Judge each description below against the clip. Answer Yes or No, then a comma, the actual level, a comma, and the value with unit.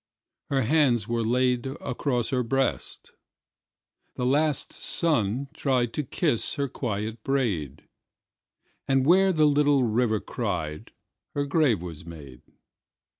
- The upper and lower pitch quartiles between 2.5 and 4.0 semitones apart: No, average, 4.6 semitones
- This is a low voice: Yes, low, 125 Hz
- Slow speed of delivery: Yes, slow, 100 wpm